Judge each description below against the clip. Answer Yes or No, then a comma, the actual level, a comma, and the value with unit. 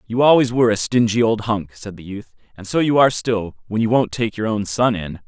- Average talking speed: No, fast, 260 wpm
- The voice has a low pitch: Yes, low, 110 Hz